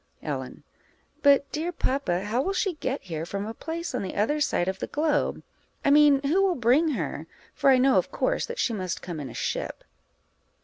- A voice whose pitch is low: No, very high, 275 Hz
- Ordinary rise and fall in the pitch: No, wide, 7.2 semitones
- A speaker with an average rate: No, fast, 210 wpm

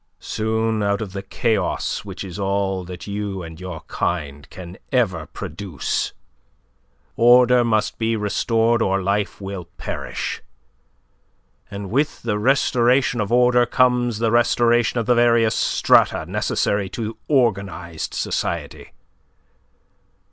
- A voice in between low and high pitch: No, low, 110 Hz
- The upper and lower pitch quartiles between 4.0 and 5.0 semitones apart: No, average, 3.6 semitones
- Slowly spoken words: Yes, slow, 120 wpm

